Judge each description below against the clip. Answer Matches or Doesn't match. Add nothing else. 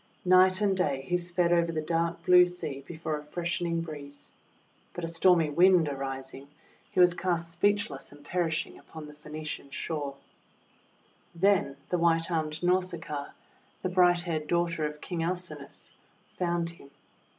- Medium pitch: Matches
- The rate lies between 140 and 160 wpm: Matches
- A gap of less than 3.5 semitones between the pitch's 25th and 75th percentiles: Matches